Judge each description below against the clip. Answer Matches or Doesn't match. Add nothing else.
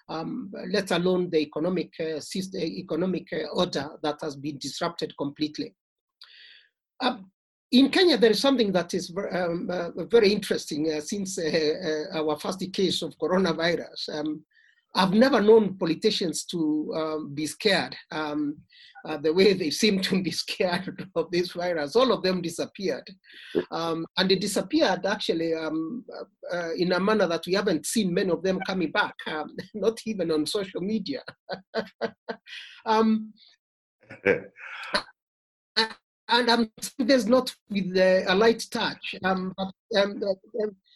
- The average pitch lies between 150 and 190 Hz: Matches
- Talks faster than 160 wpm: Doesn't match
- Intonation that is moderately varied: Matches